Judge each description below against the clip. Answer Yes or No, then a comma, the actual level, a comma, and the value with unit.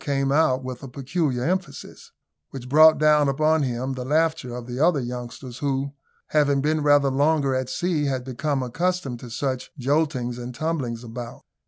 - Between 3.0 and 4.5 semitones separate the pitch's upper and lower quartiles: Yes, average, 3.4 semitones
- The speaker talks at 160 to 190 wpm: Yes, average, 170 wpm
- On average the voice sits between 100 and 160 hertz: Yes, low, 135 Hz